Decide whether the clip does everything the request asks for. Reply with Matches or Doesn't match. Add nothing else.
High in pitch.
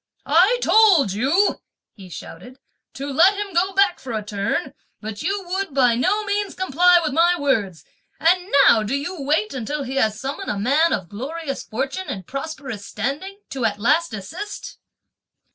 Matches